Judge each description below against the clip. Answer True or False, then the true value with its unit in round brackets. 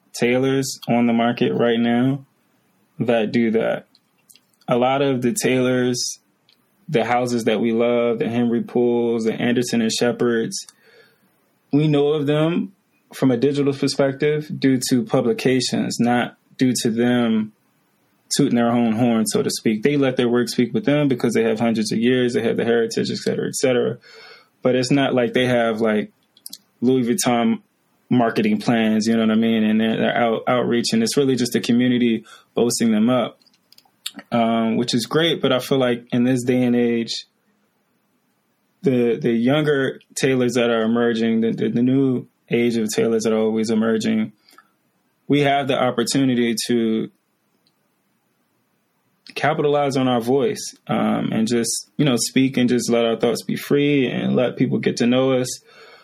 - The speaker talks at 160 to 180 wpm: True (170 wpm)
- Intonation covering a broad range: False (2.4 semitones)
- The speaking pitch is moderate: False (120 Hz)